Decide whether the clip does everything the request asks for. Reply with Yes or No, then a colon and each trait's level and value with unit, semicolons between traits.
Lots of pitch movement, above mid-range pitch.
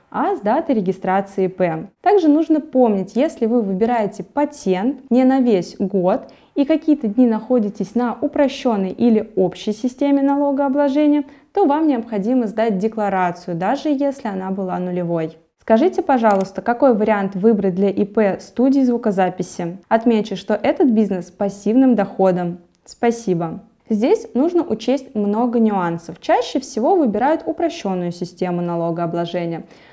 Yes: wide, 6.4 semitones; high, 220 Hz